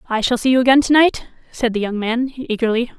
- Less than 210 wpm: No, fast, 240 wpm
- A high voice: Yes, high, 240 Hz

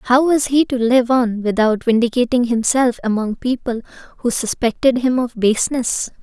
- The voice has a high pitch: Yes, high, 240 Hz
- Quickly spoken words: No, average, 155 wpm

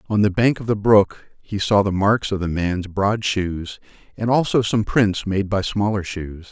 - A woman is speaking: No, male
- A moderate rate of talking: No, fast, 210 wpm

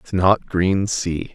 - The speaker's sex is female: No, male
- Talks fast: No, slow, 135 wpm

